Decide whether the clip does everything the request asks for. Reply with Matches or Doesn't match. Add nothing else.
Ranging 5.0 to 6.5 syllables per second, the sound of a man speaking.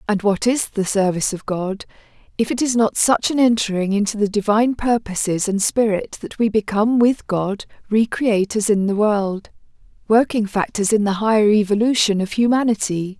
Doesn't match